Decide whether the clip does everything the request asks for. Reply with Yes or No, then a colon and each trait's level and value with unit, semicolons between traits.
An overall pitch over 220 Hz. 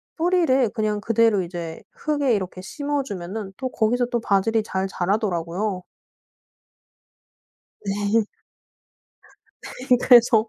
No: high, 215 Hz